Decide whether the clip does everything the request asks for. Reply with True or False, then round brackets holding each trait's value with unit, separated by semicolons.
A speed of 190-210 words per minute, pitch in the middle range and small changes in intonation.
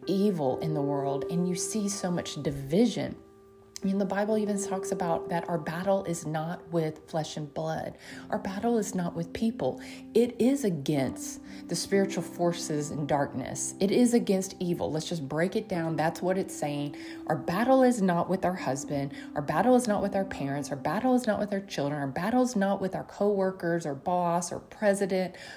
False (200 wpm; 180 Hz; 4.5 semitones)